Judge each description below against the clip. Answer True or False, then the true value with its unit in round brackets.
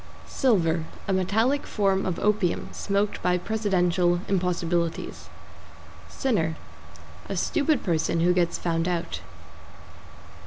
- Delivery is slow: True (105 wpm)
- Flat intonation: False (3.2 semitones)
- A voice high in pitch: False (180 Hz)